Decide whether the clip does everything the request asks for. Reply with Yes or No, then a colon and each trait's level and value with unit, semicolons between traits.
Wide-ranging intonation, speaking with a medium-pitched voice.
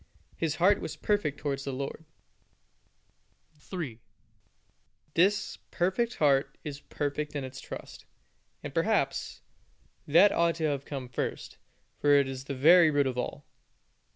No: average, 3.6 semitones; medium, 145 Hz